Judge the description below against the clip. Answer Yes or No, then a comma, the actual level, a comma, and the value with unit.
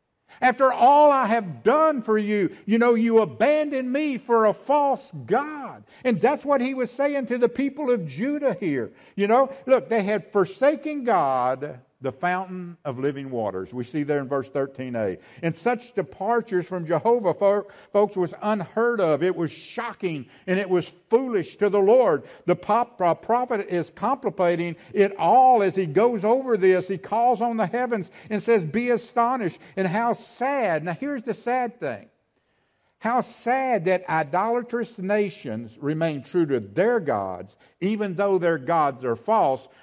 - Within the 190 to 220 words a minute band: No, average, 165 wpm